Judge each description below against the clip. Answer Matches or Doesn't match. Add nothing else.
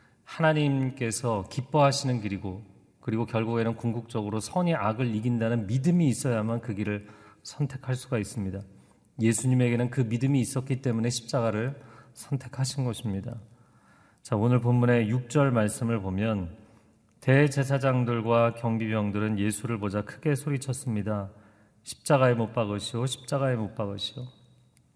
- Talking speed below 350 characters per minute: Matches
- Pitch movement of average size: Matches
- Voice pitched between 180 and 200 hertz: Doesn't match